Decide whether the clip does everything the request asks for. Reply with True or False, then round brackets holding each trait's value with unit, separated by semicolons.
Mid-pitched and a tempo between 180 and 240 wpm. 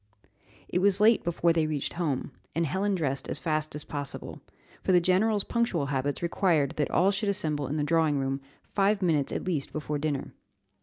True (160 Hz; 190 wpm)